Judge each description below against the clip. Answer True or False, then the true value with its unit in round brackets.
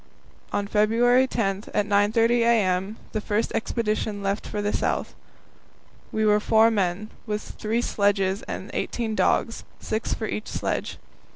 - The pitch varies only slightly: True (1.9 semitones)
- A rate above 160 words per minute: False (145 wpm)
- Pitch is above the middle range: True (215 Hz)